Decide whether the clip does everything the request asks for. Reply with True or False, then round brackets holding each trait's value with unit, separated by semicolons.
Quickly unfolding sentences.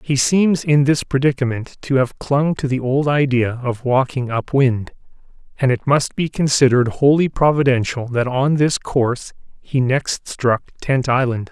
False (165 wpm)